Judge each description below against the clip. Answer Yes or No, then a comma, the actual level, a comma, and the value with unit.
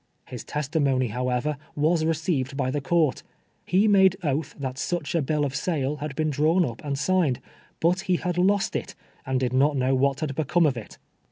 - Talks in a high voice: No, medium, 150 Hz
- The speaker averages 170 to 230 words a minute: Yes, average, 200 wpm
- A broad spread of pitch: No, average, 4.2 semitones